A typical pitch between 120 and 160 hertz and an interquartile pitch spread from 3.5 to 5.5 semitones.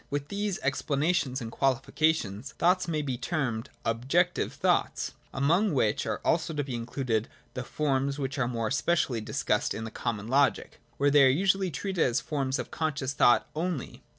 Yes: medium, 140 Hz; average, 4.5 semitones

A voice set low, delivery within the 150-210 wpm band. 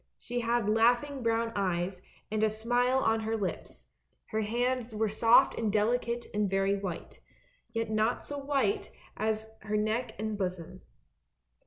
No: high, 220 Hz; average, 155 wpm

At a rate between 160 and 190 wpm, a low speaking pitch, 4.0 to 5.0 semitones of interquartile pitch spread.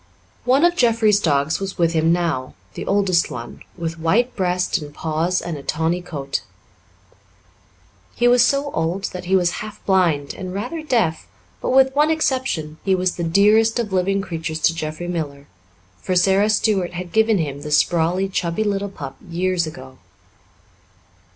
No: average, 165 wpm; medium, 180 Hz; average, 4.4 semitones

